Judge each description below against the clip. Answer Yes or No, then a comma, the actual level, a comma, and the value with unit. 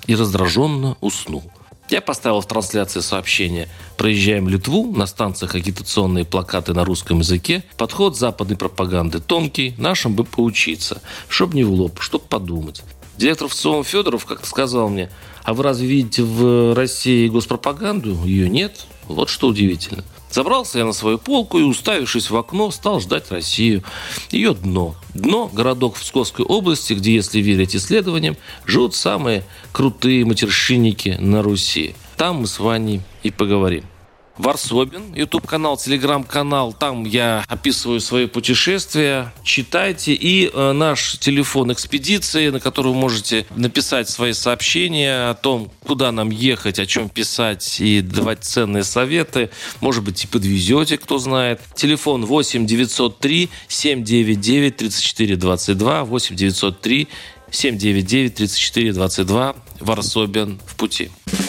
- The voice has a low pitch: Yes, low, 115 Hz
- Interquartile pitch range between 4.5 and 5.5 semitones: Yes, average, 5.2 semitones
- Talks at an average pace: Yes, average, 135 wpm